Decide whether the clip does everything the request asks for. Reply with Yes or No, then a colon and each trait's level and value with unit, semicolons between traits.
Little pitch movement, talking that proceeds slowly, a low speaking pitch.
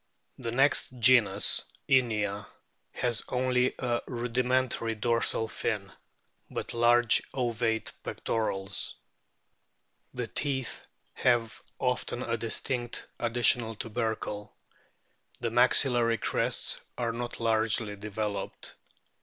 Yes: narrow, 2.0 semitones; slow, 90 wpm; low, 115 Hz